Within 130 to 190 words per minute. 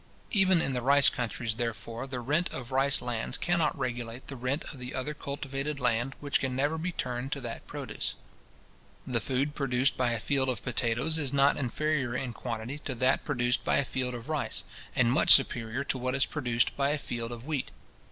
No: average, 200 wpm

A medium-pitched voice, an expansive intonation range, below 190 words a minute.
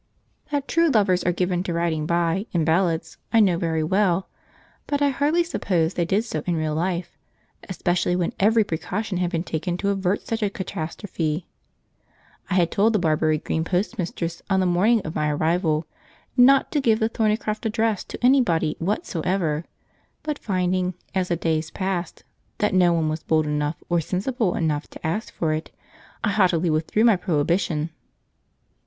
No: medium, 180 Hz; average, 4.2 semitones; average, 170 wpm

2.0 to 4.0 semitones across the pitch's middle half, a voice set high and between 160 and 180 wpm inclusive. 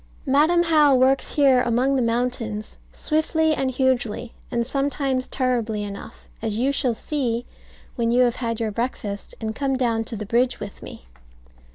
Yes: average, 2.9 semitones; very high, 250 Hz; average, 165 wpm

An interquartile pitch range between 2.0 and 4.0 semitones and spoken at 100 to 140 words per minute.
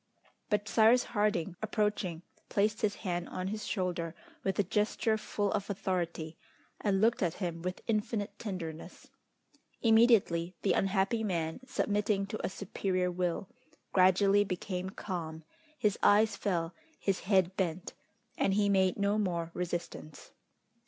Yes: average, 2.9 semitones; slow, 135 wpm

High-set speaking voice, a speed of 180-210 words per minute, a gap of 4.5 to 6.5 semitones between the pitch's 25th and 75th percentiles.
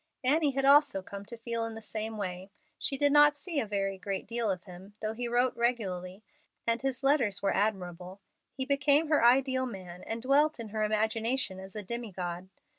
Yes: high, 225 Hz; average, 200 wpm; average, 5.2 semitones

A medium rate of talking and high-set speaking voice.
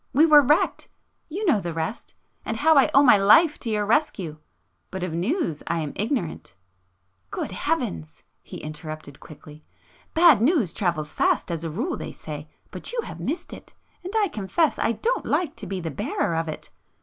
Yes: average, 185 wpm; high, 200 Hz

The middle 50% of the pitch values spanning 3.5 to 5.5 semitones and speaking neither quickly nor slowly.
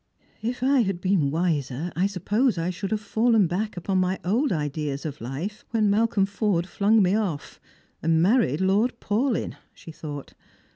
Yes: average, 4.9 semitones; average, 175 wpm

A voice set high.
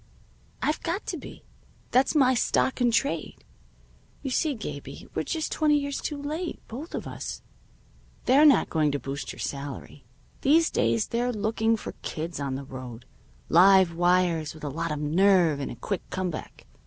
Yes: high, 195 Hz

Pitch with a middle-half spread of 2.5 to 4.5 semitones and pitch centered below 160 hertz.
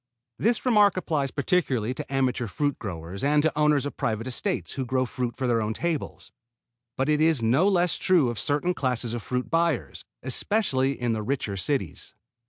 No: average, 5.0 semitones; low, 135 Hz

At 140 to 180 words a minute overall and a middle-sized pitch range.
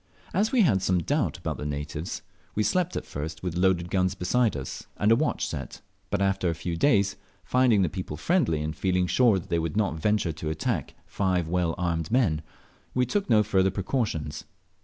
No: average, 200 wpm; average, 4.8 semitones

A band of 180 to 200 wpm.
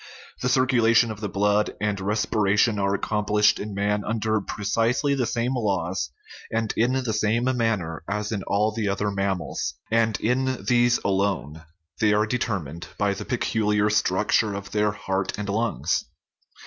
No: average, 155 wpm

